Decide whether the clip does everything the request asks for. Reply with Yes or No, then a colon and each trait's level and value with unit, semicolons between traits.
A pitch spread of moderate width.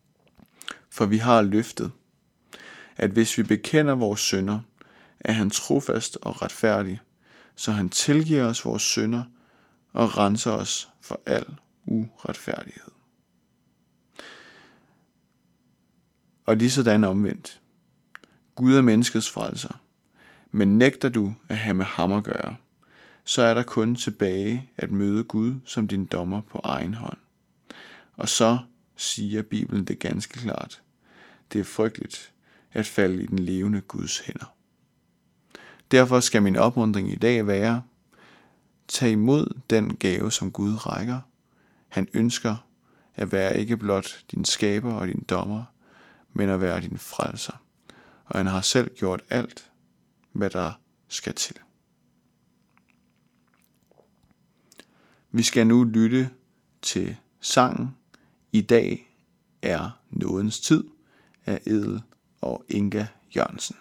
Yes: average, 3.0 semitones